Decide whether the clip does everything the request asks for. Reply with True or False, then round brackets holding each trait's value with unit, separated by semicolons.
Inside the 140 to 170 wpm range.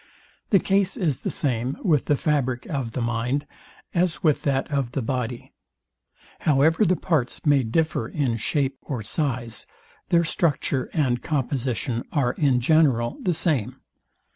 True (145 wpm)